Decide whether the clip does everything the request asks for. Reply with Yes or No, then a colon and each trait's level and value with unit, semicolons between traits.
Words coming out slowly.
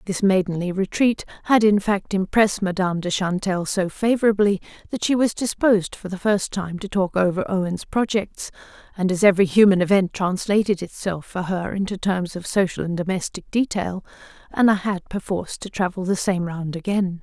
No: average, 175 wpm